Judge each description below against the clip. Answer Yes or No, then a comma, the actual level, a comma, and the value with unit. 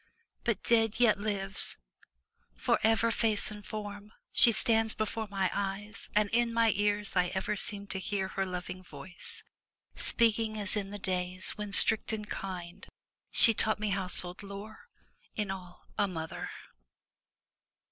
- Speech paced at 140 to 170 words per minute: Yes, average, 150 wpm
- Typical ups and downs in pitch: No, narrow, 2.3 semitones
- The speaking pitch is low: No, high, 205 Hz